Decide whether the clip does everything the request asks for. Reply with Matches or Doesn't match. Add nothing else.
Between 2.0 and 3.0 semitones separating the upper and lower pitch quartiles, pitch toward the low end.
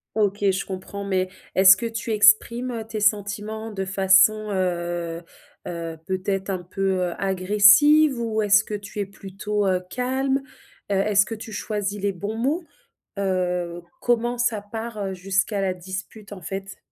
Doesn't match